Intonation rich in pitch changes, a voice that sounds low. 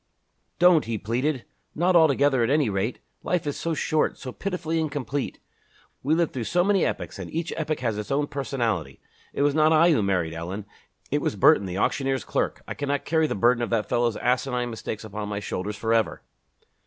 Yes: wide, 6.1 semitones; low, 130 Hz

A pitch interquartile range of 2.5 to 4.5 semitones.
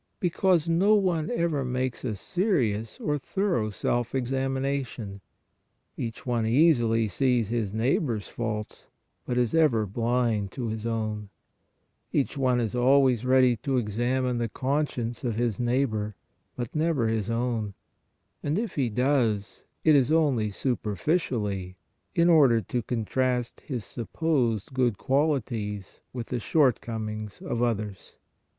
Yes: average, 3.7 semitones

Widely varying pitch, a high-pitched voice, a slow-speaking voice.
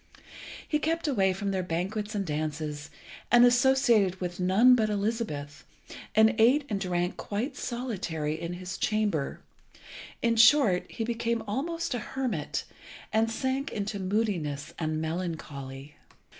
Yes: wide, 5.8 semitones; high, 205 Hz; slow, 130 wpm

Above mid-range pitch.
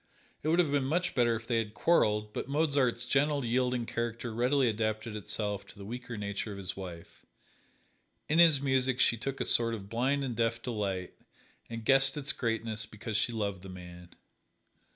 No: low, 115 Hz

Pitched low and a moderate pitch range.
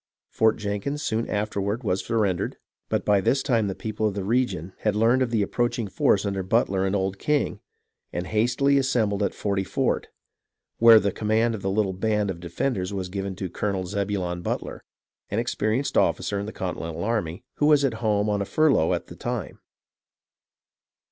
Yes: low, 105 Hz; average, 3.1 semitones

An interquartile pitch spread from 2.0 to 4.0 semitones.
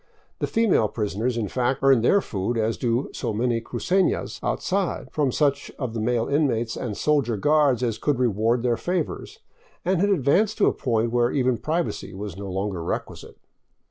No: average, 4.7 semitones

